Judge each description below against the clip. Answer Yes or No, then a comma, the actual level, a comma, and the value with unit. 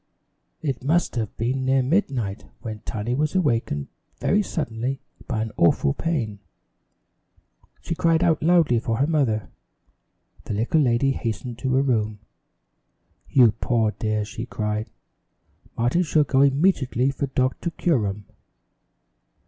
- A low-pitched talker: Yes, low, 125 Hz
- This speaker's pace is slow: Yes, slow, 130 wpm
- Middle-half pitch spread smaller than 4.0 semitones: No, average, 4.9 semitones